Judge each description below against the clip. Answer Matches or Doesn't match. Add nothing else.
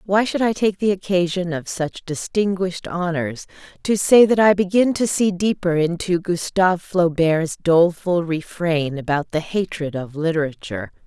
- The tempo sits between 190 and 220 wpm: Doesn't match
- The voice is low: Doesn't match